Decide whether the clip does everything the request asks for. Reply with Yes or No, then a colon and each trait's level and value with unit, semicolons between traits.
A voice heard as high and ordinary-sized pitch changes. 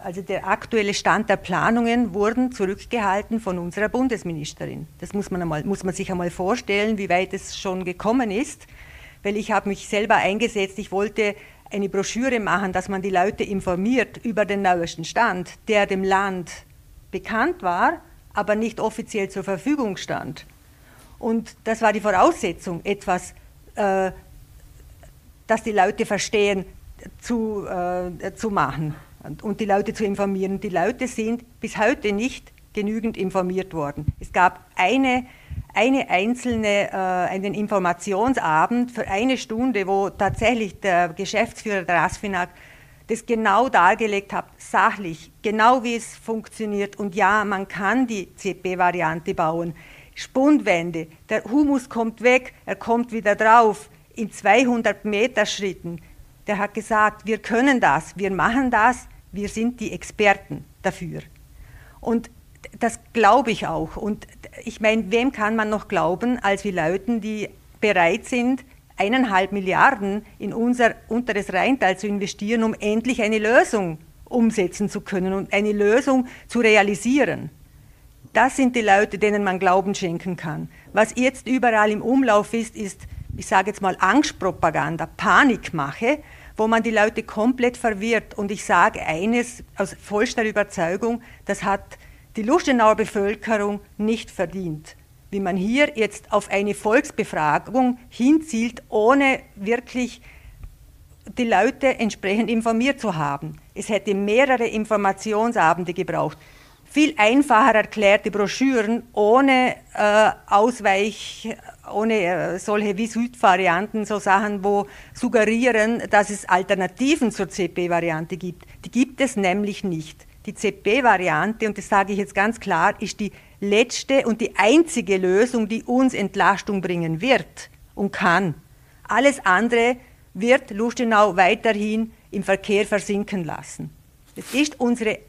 Yes: high, 210 Hz; average, 3.2 semitones